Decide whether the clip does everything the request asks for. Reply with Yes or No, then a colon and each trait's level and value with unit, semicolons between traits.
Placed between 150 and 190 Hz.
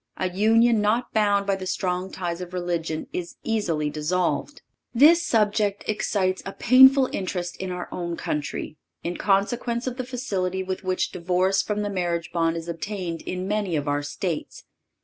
Yes: medium, 185 Hz